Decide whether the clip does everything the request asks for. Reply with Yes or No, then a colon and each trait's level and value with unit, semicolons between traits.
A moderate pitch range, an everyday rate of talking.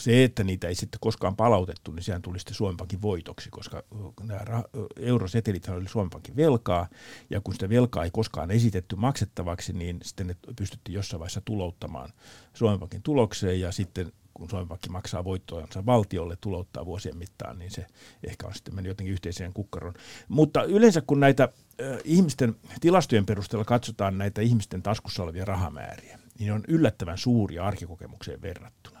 No: average, 4.2 semitones; fast, 160 wpm